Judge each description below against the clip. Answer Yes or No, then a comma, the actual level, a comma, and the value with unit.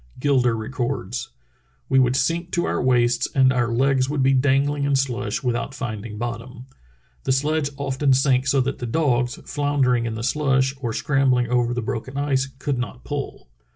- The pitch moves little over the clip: Yes, narrow, 2.2 semitones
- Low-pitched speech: Yes, low, 130 Hz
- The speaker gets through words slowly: No, average, 180 wpm